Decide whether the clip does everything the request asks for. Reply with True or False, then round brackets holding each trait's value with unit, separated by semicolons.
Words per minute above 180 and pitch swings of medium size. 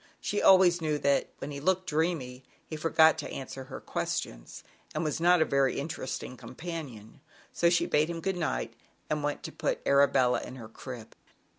True (190 wpm; 4.3 semitones)